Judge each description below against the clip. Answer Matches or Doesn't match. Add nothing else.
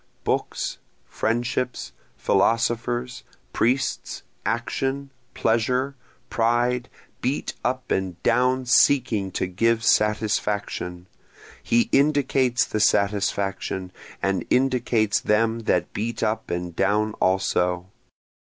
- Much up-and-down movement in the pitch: Doesn't match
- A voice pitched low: Matches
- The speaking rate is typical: Doesn't match